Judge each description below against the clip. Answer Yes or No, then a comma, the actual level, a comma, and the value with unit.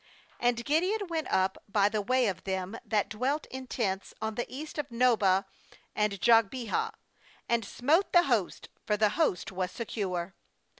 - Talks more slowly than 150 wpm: No, average, 160 wpm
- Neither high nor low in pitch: No, high, 225 Hz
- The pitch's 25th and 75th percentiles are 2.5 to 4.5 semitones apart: No, average, 4.9 semitones